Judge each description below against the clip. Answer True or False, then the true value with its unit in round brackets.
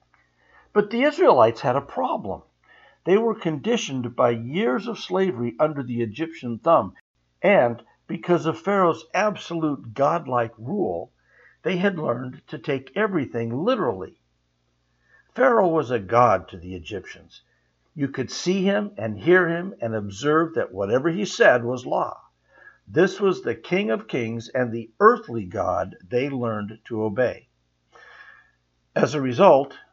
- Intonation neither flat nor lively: False (8.1 semitones)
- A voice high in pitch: False (135 Hz)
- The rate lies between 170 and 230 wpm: False (140 wpm)